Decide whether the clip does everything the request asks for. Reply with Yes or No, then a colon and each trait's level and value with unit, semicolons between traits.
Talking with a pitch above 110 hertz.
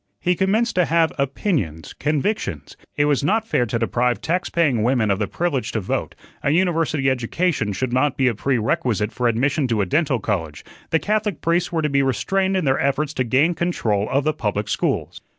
Yes: medium, 140 Hz